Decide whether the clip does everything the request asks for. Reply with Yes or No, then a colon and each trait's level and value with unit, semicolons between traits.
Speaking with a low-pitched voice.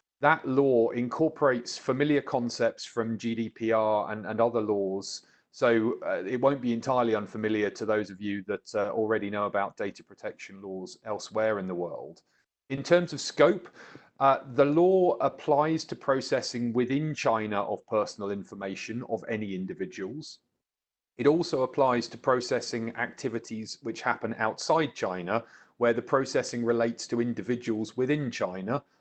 Yes: low, 115 Hz